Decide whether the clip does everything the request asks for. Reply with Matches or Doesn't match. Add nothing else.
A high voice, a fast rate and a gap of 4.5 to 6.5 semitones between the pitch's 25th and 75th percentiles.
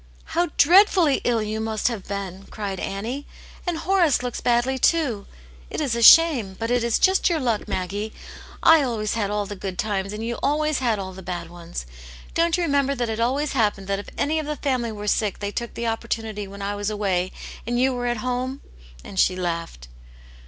Matches